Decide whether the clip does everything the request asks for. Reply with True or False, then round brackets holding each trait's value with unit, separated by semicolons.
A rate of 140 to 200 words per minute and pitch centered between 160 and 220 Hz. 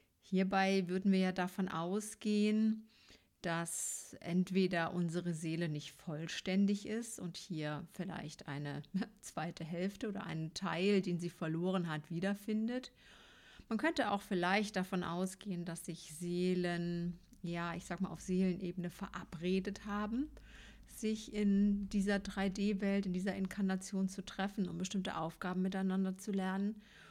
False (130 wpm; 190 Hz)